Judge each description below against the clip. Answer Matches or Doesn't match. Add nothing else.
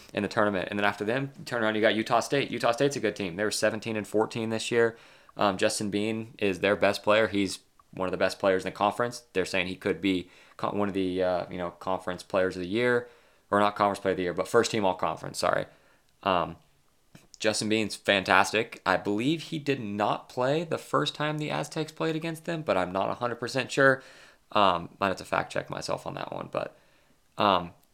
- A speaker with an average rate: Doesn't match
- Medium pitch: Doesn't match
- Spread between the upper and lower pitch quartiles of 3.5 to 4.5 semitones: Matches